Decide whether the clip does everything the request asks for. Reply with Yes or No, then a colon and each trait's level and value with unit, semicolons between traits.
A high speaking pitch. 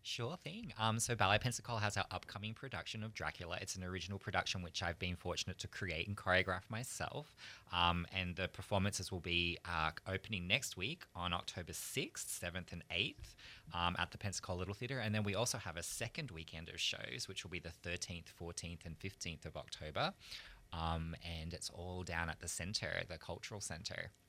No: very low, 95 Hz